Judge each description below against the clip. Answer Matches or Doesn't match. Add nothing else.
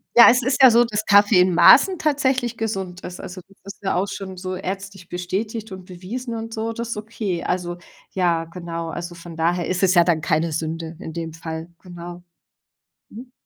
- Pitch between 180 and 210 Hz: Matches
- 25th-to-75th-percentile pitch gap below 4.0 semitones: Doesn't match